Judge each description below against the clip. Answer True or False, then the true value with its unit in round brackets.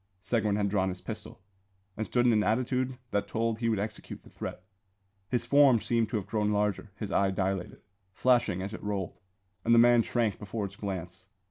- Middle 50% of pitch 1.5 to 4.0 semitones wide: True (3.0 semitones)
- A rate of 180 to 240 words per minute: True (200 wpm)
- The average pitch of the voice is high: False (105 Hz)